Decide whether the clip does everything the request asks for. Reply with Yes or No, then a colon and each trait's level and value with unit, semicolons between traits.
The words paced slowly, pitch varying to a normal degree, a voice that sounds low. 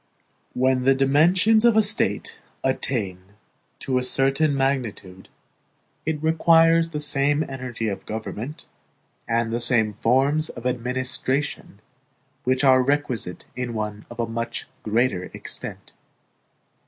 Yes: slow, 115 wpm; average, 4.1 semitones; low, 130 Hz